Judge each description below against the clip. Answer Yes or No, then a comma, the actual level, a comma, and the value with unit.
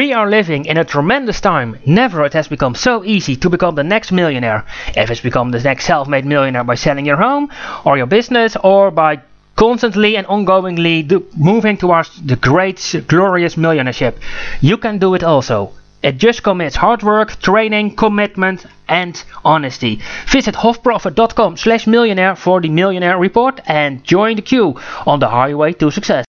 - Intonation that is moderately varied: No, wide, 6.4 semitones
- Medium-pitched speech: Yes, medium, 180 Hz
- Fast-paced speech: No, average, 165 wpm